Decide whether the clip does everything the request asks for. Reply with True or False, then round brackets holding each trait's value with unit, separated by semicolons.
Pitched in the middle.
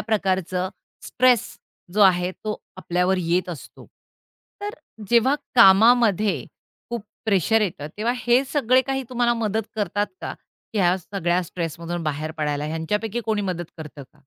False (195 Hz)